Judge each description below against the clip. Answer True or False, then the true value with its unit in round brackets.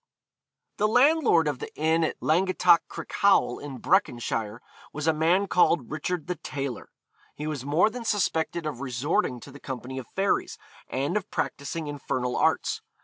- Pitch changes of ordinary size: True (4.8 semitones)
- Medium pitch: True (155 Hz)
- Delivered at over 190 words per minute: False (155 wpm)